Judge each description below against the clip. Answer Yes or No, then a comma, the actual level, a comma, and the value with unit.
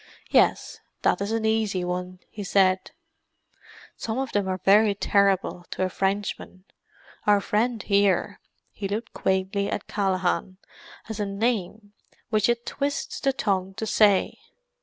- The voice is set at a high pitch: Yes, high, 200 Hz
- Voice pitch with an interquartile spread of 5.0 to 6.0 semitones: No, narrow, 2.5 semitones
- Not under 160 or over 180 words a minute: No, slow, 135 wpm